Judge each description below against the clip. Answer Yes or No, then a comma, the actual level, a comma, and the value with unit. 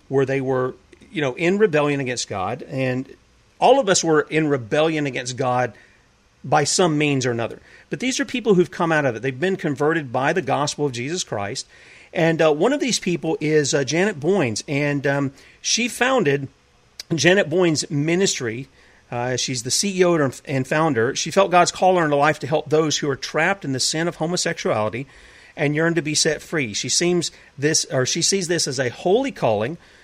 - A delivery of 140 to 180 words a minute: No, average, 200 wpm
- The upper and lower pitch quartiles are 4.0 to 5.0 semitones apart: Yes, average, 4.5 semitones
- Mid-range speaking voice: Yes, medium, 150 Hz